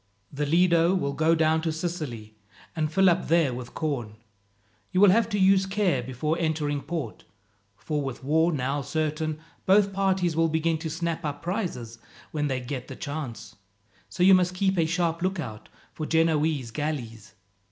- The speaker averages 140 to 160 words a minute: No, average, 170 wpm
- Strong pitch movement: No, average, 3.7 semitones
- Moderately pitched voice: Yes, medium, 160 Hz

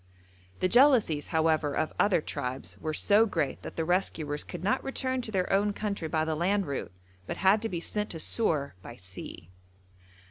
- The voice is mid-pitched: Yes, medium, 175 Hz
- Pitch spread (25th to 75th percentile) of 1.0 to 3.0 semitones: No, average, 5.2 semitones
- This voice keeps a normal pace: Yes, average, 185 wpm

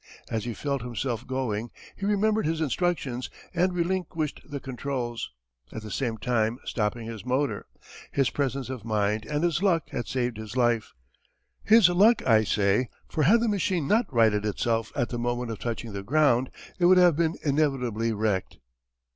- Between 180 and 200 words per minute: No, average, 170 wpm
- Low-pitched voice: Yes, low, 125 Hz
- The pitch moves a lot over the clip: Yes, wide, 6.1 semitones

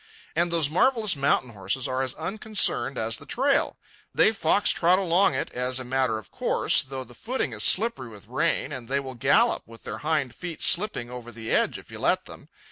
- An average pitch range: No, wide, 6.5 semitones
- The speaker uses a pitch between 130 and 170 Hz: Yes, low, 135 Hz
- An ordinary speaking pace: No, fast, 210 wpm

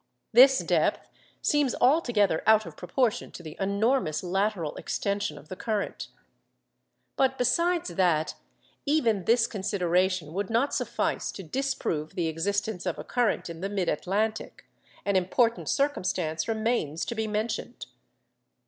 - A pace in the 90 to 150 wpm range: Yes, slow, 135 wpm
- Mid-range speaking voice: No, high, 205 Hz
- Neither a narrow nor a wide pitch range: Yes, average, 5.0 semitones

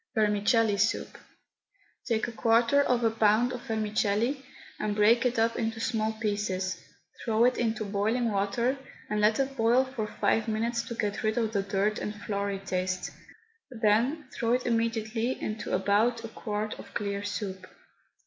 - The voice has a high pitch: Yes, high, 220 Hz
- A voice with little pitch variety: Yes, narrow, 2.2 semitones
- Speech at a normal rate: Yes, average, 160 wpm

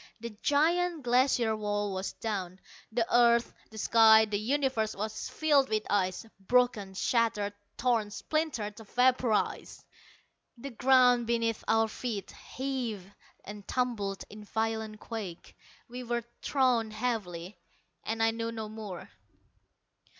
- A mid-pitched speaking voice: No, high, 225 Hz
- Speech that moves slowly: Yes, slow, 120 wpm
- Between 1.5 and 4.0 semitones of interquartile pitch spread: Yes, average, 2.9 semitones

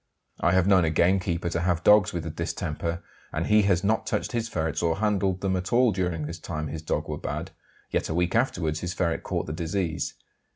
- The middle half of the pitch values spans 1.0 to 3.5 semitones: Yes, average, 3.0 semitones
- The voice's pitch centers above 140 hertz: No, very low, 90 Hz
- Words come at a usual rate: No, fast, 220 wpm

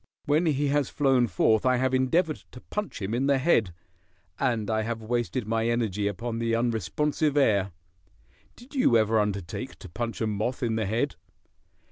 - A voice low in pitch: Yes, low, 120 Hz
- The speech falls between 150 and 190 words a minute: Yes, average, 175 wpm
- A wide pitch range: No, average, 3.9 semitones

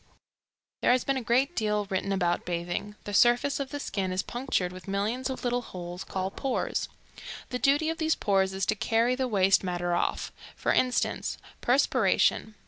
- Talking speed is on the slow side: No, average, 180 wpm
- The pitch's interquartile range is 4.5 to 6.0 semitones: Yes, average, 5.2 semitones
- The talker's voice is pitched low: No, high, 215 Hz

